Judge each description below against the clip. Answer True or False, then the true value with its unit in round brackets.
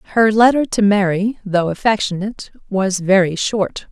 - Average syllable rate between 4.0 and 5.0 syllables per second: True (4.8 syllables/s)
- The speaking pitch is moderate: False (200 Hz)